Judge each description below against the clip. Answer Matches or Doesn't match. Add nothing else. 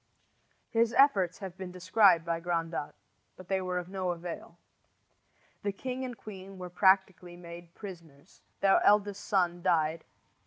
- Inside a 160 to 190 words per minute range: Doesn't match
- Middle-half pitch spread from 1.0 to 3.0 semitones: Matches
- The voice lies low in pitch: Doesn't match